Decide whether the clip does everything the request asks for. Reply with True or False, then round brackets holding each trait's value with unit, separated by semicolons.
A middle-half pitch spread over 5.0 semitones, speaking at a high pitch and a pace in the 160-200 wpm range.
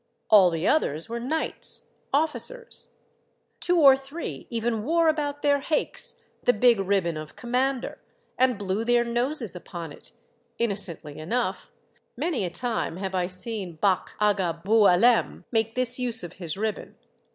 False (5.6 semitones; 225 Hz; 145 wpm)